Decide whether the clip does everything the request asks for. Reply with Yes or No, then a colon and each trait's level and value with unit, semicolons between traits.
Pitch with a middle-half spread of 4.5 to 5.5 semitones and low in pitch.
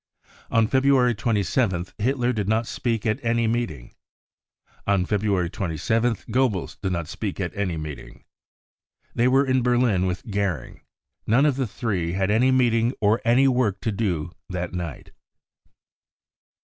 Yes: average, 4.8 semitones; low, 110 Hz